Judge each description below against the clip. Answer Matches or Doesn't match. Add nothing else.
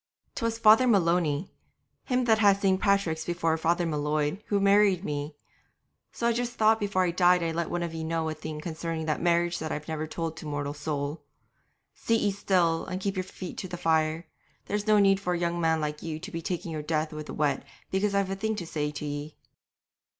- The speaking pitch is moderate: Matches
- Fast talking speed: Matches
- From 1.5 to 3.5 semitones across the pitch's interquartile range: Doesn't match